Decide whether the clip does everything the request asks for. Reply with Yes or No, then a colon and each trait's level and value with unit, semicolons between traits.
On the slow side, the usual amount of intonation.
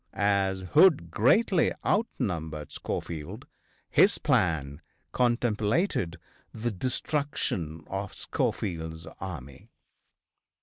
No: slow, 75 wpm; wide, 6.9 semitones